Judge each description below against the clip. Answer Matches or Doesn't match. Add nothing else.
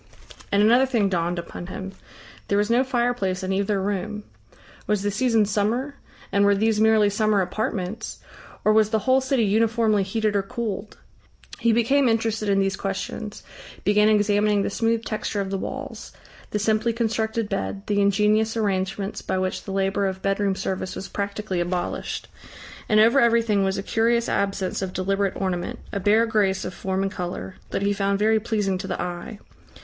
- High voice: Matches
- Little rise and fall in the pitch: Matches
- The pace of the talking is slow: Doesn't match